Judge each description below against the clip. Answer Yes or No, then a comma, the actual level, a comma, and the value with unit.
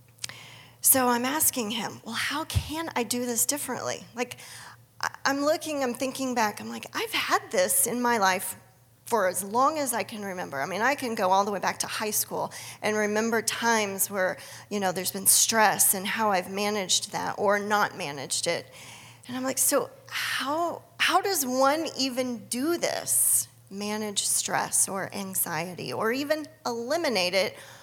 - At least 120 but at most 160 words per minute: No, average, 175 wpm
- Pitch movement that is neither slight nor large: No, wide, 5.8 semitones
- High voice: Yes, high, 210 Hz